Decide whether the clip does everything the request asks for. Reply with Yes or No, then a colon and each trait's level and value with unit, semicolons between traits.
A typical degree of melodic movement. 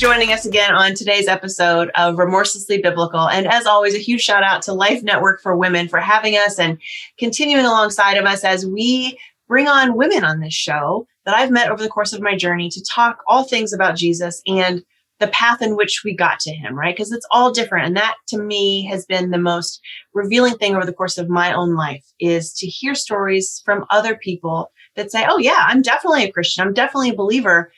Yes: average, 4.0 semitones